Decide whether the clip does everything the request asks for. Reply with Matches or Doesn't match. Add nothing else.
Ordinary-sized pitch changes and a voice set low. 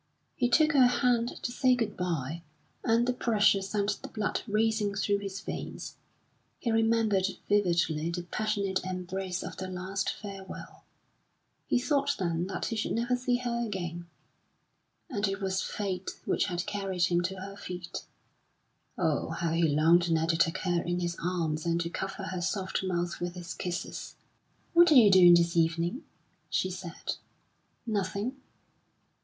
Doesn't match